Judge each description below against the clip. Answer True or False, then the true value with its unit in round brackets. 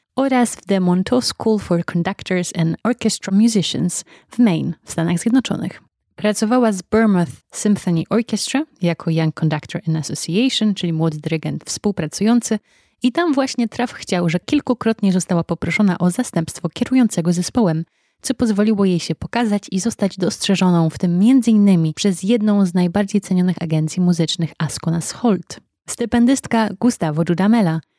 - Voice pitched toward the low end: False (195 Hz)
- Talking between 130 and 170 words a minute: True (140 wpm)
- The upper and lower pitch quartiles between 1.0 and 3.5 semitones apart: False (4.8 semitones)